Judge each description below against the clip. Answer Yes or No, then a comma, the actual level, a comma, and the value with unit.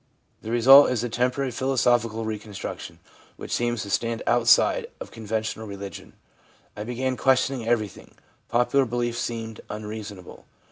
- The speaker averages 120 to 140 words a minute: Yes, slow, 135 wpm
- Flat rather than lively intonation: Yes, narrow, 2.2 semitones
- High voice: No, low, 115 Hz